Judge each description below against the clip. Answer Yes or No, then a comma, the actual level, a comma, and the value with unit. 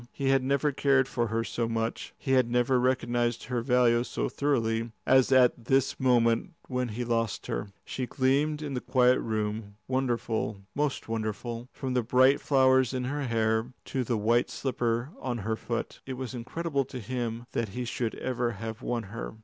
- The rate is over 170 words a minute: Yes, average, 180 wpm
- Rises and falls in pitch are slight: Yes, narrow, 2.3 semitones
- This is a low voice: Yes, low, 125 Hz